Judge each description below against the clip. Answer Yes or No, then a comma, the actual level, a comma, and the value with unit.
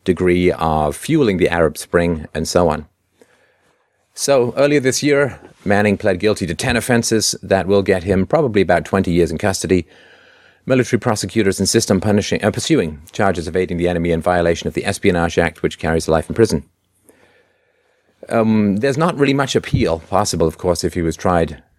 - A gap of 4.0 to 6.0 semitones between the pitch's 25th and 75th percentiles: Yes, average, 4.5 semitones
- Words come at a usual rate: Yes, average, 180 wpm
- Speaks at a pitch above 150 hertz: No, very low, 95 Hz